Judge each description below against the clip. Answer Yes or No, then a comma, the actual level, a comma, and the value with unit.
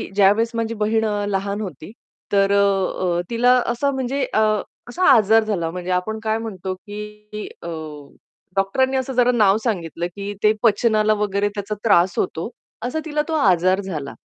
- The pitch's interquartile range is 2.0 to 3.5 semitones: Yes, average, 2.9 semitones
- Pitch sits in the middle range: No, high, 210 Hz